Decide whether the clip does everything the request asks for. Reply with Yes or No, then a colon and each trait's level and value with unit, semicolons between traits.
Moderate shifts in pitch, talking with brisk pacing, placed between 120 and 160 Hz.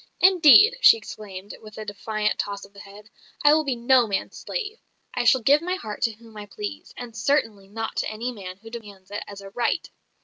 No: average, 4.6 semitones; fast, 215 wpm; high, 225 Hz